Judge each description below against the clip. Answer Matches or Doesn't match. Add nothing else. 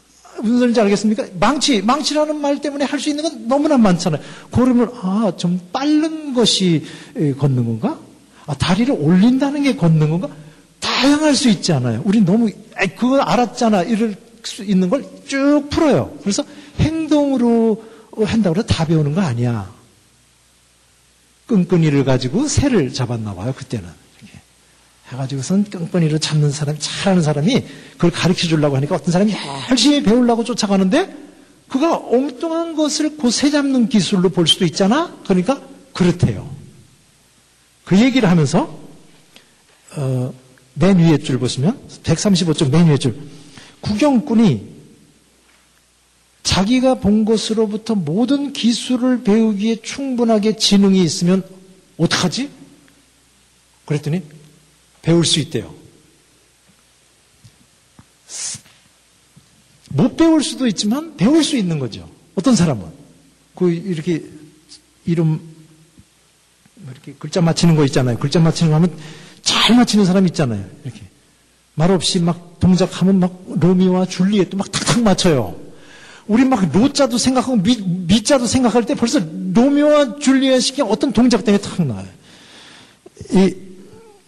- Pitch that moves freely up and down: Matches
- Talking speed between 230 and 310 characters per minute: Matches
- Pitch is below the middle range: Doesn't match